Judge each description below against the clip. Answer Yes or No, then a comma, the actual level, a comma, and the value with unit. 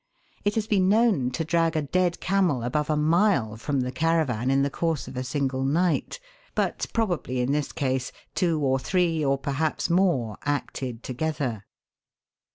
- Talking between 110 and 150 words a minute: No, average, 165 wpm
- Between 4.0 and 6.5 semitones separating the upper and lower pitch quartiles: Yes, average, 4.7 semitones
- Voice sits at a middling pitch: Yes, medium, 150 Hz